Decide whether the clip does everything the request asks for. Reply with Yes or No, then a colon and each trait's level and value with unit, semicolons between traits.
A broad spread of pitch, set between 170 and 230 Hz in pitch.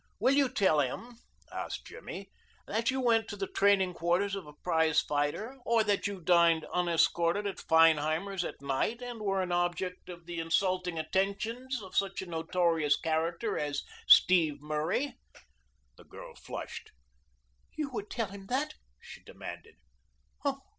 No: average, 4.2 semitones; medium, 185 Hz